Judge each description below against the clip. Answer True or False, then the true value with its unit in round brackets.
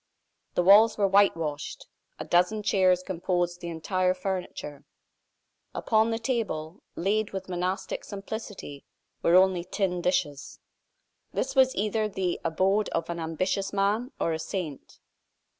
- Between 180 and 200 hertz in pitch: True (185 Hz)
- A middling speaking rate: False (130 wpm)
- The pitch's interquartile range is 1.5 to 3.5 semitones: True (3.0 semitones)